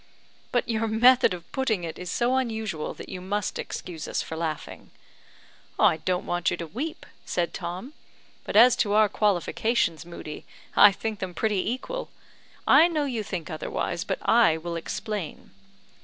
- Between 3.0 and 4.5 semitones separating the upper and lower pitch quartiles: No, average, 5.2 semitones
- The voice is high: Yes, high, 205 Hz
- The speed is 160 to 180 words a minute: Yes, average, 165 wpm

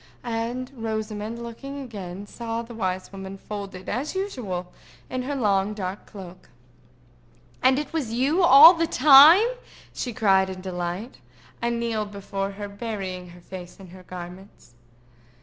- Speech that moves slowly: No, average, 145 wpm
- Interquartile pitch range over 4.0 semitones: Yes, average, 4.8 semitones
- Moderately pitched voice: No, high, 210 Hz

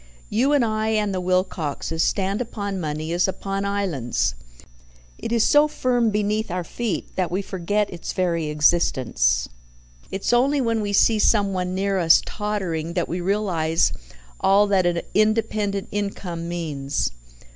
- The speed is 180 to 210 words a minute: No, average, 145 wpm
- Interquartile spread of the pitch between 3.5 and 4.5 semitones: Yes, average, 3.8 semitones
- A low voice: No, high, 195 Hz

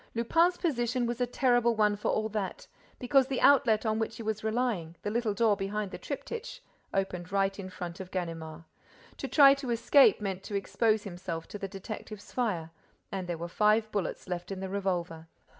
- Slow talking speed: No, average, 190 wpm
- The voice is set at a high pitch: Yes, high, 210 Hz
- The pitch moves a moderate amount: Yes, average, 4.1 semitones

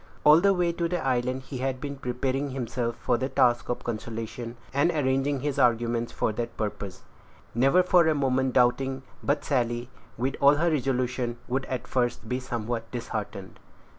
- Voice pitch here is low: Yes, low, 130 Hz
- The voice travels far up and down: No, average, 2.7 semitones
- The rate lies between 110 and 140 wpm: No, average, 170 wpm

